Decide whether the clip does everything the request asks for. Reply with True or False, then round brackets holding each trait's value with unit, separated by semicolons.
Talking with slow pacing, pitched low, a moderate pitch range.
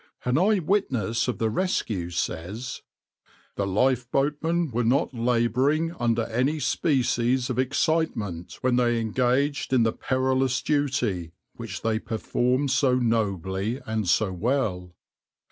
True (130 wpm; 125 Hz; 3.6 semitones)